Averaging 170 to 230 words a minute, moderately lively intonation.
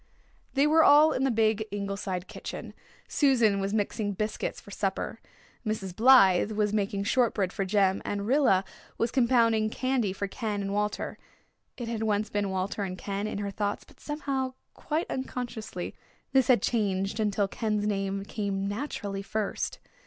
No: average, 160 wpm; average, 3.0 semitones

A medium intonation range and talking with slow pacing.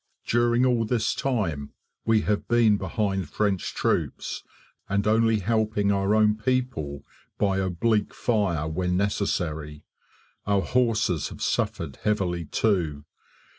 Yes: average, 3.9 semitones; slow, 120 wpm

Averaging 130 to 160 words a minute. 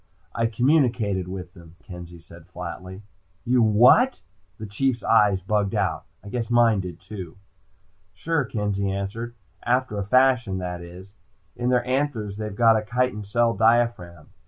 Yes: average, 150 wpm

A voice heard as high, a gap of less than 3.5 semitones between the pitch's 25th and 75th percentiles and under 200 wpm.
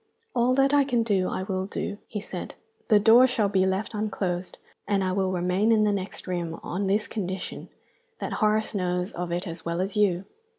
No: high, 195 Hz; average, 2.8 semitones; fast, 205 wpm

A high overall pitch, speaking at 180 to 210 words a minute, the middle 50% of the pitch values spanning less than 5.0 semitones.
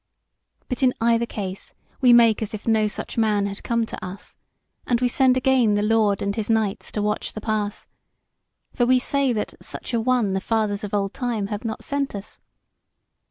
Yes: high, 220 Hz; average, 200 wpm; average, 2.7 semitones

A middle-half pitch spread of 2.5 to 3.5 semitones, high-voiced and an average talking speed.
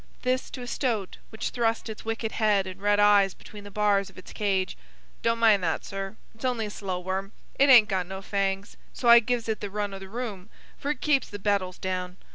No: average, 2.8 semitones; high, 205 Hz; fast, 230 wpm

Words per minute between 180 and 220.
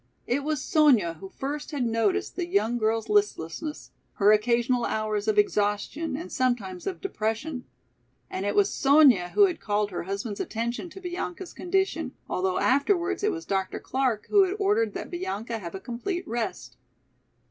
No: average, 165 wpm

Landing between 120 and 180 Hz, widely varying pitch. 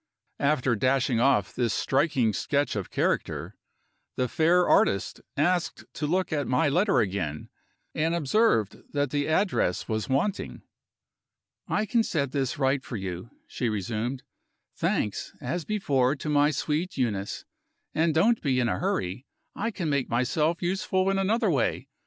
Yes: medium, 140 Hz; wide, 6.1 semitones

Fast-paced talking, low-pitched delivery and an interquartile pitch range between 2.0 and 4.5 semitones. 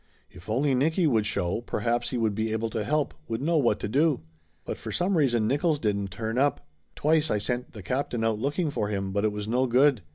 No: fast, 230 wpm; low, 120 Hz; average, 5.1 semitones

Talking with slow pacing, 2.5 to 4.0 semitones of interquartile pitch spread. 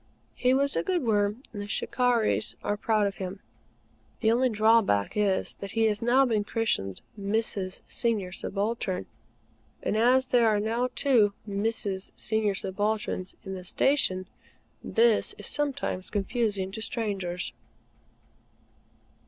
Yes: slow, 130 wpm; average, 2.9 semitones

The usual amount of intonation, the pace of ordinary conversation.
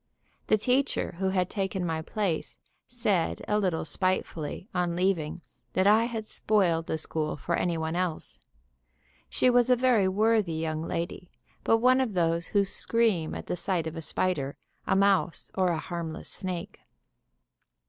Yes: average, 4.3 semitones; average, 160 wpm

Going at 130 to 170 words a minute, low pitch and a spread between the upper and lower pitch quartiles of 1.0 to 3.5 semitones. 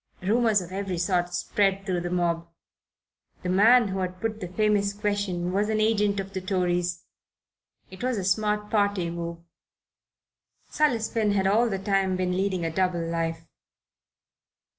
No: average, 160 wpm; high, 190 Hz; average, 2.8 semitones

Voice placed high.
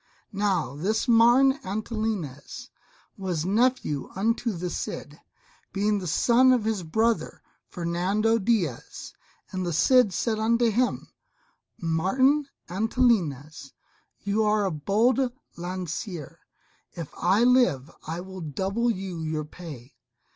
Yes: high, 195 Hz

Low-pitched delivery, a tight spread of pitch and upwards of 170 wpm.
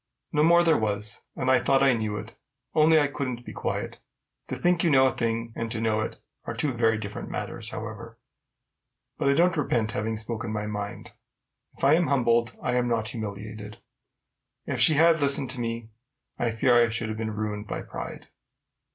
No: low, 115 Hz; average, 4.1 semitones; average, 195 wpm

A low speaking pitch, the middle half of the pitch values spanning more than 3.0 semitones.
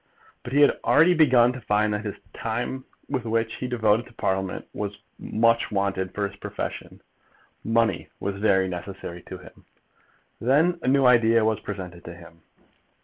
Yes: low, 110 Hz; average, 3.9 semitones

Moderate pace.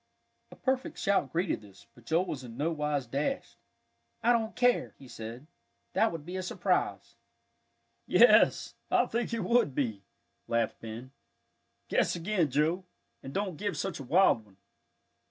Yes: average, 155 wpm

